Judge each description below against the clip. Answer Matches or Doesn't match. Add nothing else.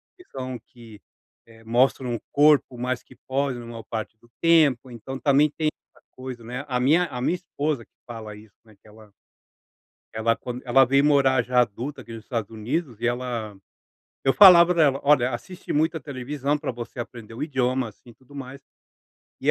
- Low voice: Matches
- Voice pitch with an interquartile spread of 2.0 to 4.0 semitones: Matches